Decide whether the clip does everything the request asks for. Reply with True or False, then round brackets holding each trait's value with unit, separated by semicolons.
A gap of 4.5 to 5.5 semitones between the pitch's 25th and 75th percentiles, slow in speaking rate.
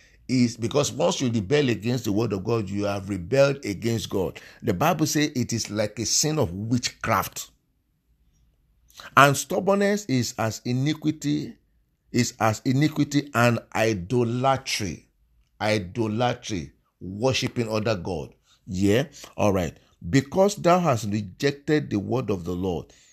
True (5.0 semitones; 130 wpm)